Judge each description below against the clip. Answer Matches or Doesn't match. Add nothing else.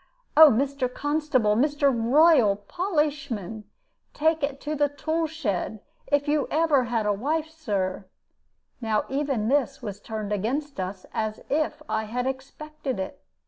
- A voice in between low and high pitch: Doesn't match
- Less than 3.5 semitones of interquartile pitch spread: Doesn't match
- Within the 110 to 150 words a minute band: Matches